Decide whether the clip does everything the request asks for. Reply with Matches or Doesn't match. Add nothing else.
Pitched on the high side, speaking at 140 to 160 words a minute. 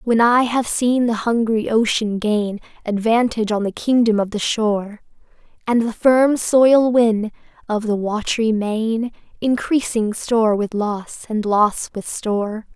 Matches